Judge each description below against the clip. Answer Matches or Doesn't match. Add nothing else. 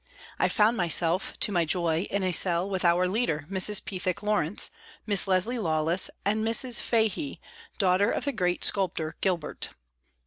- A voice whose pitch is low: Doesn't match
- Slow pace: Doesn't match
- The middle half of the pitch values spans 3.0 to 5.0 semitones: Matches